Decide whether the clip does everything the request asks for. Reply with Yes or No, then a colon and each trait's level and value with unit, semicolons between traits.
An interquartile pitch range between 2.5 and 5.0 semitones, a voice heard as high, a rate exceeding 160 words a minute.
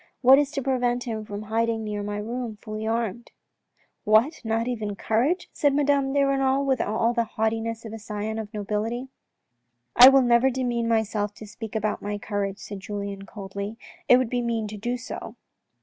Yes: average, 2.9 semitones; high, 225 Hz; fast, 205 wpm